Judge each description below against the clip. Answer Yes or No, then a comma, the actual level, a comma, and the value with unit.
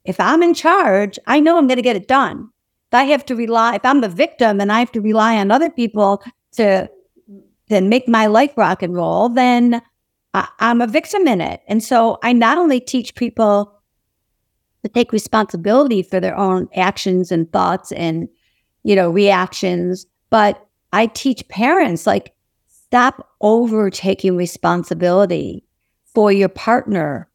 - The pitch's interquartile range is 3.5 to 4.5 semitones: Yes, average, 4.1 semitones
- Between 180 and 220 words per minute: No, average, 160 wpm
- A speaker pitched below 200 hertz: No, high, 220 Hz